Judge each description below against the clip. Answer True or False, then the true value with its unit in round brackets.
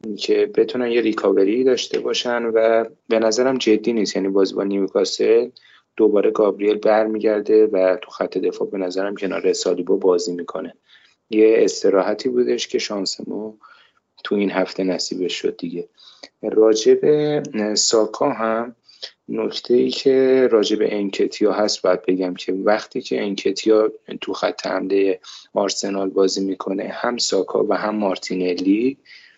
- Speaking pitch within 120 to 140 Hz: False (110 Hz)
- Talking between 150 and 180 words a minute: False (135 wpm)